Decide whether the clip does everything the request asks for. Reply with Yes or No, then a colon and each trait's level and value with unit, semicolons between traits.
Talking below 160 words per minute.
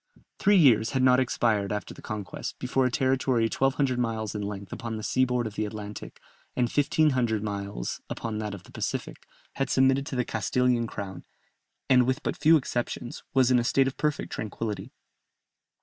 No: average, 180 wpm